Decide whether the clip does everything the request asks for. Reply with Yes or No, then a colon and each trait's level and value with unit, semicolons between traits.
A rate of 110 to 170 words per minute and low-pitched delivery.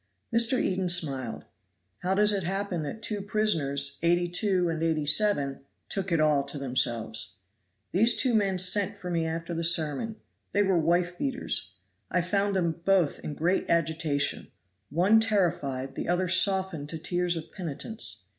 No: average, 155 wpm; medium, 175 Hz